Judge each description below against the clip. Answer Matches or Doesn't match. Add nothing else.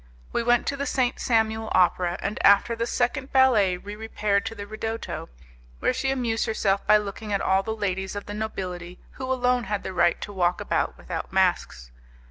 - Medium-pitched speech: Doesn't match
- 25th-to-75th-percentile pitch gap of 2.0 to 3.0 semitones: Doesn't match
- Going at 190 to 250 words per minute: Matches